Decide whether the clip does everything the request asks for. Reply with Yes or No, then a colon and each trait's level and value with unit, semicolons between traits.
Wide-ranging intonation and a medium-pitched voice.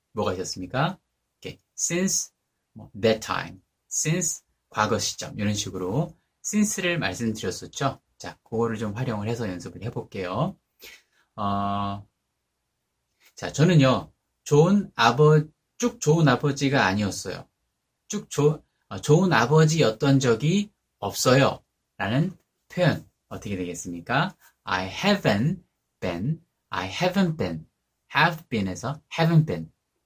No: wide, 8.4 semitones; low, 130 Hz